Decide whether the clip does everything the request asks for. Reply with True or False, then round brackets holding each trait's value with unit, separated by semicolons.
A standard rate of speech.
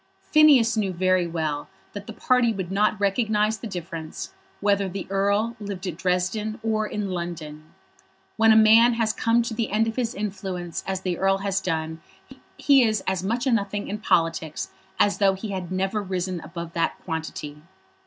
True (180 wpm)